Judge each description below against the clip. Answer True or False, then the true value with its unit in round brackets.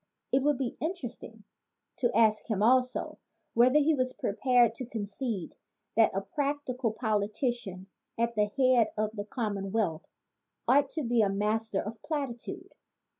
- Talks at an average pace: True (145 wpm)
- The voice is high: True (230 Hz)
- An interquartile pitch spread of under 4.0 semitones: True (3.6 semitones)